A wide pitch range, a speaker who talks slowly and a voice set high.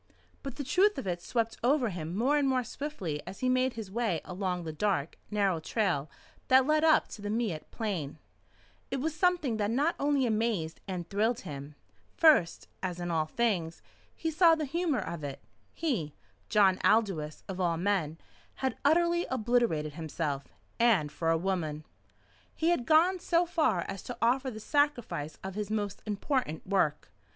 No: wide, 7.8 semitones; average, 175 wpm; high, 215 Hz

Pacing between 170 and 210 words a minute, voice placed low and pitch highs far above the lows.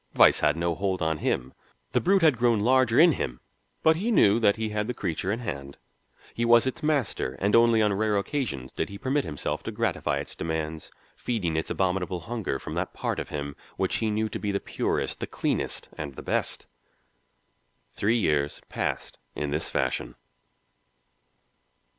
Yes: average, 185 wpm; low, 100 Hz; wide, 7.0 semitones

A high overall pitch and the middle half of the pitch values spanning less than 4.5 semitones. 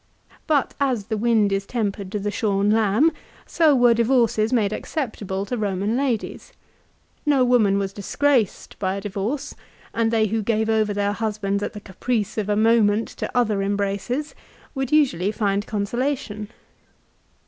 Yes: high, 215 Hz; average, 3.1 semitones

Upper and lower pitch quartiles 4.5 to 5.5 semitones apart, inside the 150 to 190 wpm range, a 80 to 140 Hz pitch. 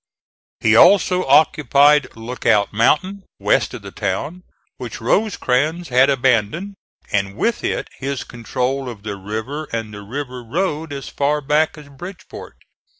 No: average, 5.1 semitones; average, 140 wpm; low, 135 Hz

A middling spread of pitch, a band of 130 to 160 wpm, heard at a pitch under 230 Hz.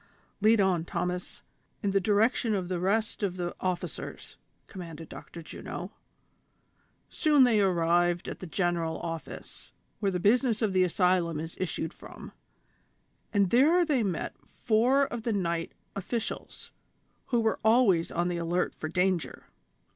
Yes: average, 4.2 semitones; average, 145 wpm; medium, 185 Hz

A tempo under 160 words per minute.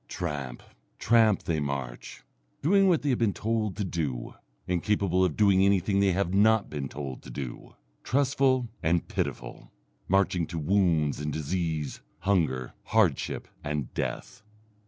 Yes: average, 140 wpm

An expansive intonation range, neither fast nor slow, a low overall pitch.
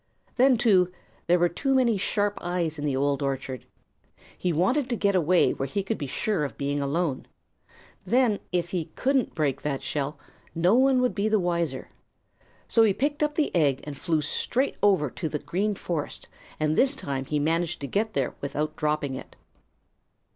No: wide, 6.6 semitones; average, 185 wpm; medium, 175 Hz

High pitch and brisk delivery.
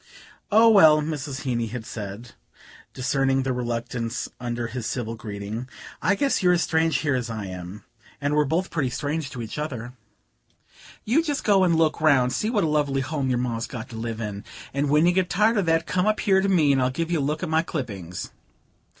No: medium, 140 Hz; fast, 220 wpm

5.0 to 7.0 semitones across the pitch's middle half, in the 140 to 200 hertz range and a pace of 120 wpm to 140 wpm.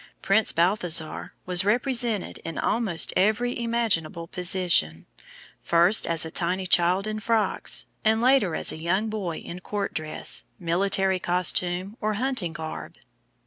No: average, 4.1 semitones; medium, 185 Hz; slow, 135 wpm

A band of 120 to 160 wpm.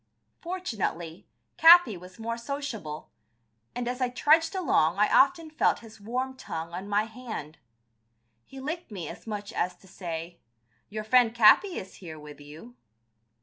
Yes: average, 150 wpm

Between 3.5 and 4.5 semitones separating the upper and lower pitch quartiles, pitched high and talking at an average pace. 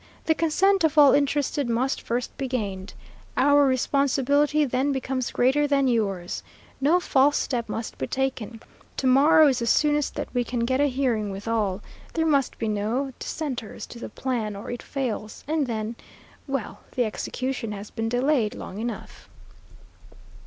Yes: average, 4.0 semitones; very high, 255 Hz; average, 165 wpm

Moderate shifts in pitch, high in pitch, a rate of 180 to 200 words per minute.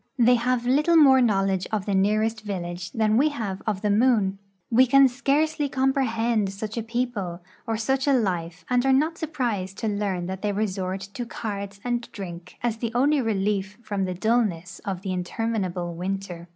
Yes: average, 4.3 semitones; high, 215 Hz; average, 185 wpm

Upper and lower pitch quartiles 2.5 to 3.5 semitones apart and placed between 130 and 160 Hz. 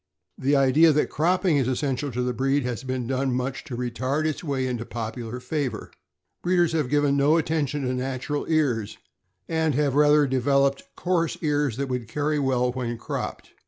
Yes: average, 2.9 semitones; low, 135 Hz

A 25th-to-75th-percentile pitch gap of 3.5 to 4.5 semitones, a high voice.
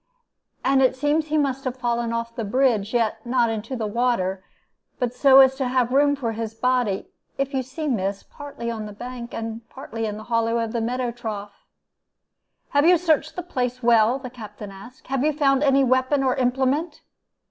No: average, 3.0 semitones; very high, 250 Hz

